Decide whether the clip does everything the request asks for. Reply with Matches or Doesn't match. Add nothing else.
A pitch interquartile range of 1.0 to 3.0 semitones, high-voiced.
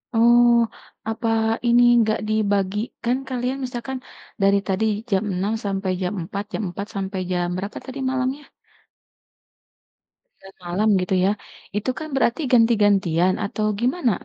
Doesn't match